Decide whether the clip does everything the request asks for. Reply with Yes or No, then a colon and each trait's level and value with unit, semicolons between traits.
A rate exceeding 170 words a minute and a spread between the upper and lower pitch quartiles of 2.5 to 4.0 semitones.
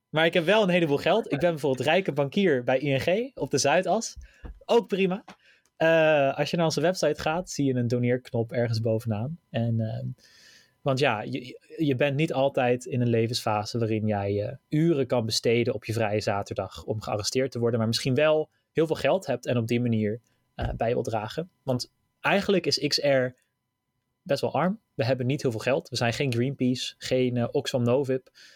No: fast, 200 wpm; average, 4.5 semitones